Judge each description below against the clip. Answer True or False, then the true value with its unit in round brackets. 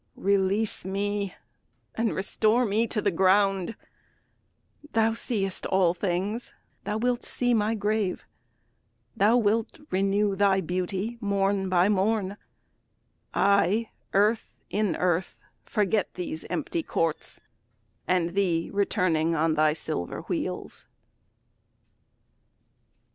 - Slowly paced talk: True (105 wpm)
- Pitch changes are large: False (2.7 semitones)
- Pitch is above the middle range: True (200 Hz)